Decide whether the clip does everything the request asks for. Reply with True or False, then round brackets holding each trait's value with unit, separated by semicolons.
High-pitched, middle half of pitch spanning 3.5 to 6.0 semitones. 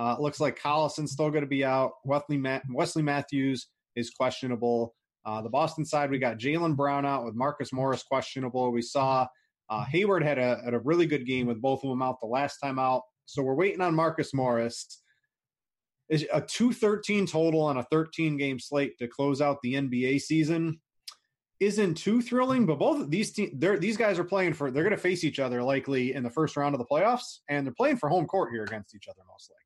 False (140 Hz; 3.8 semitones)